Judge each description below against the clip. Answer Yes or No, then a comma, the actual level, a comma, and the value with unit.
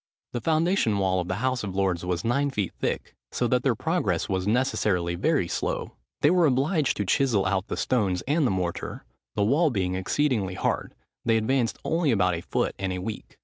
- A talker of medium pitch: No, low, 105 Hz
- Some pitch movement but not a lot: No, wide, 6.6 semitones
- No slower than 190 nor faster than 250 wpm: Yes, average, 200 wpm